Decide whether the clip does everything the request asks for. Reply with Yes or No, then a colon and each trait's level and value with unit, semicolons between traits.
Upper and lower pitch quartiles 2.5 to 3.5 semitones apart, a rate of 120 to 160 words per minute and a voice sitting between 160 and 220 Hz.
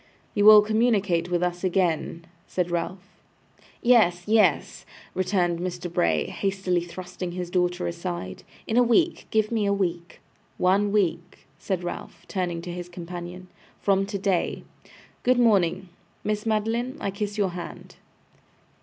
Yes: average, 2.9 semitones; slow, 135 wpm; medium, 185 Hz